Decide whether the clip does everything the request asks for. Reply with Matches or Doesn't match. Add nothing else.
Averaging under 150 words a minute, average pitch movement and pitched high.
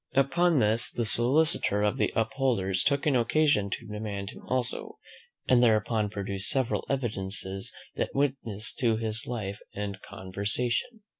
Doesn't match